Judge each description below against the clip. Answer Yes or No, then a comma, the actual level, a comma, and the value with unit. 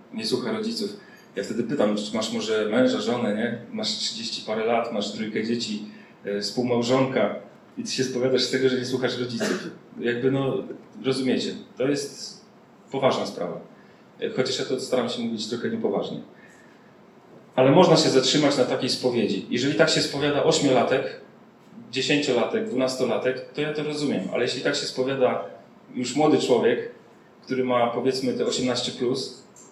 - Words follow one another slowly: No, average, 155 wpm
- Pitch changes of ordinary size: Yes, average, 4.2 semitones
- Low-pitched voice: Yes, low, 130 Hz